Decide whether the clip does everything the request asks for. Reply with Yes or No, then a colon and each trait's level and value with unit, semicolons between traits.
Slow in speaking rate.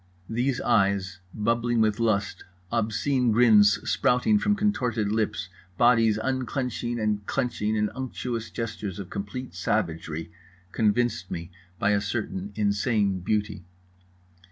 Yes: slow, 115 wpm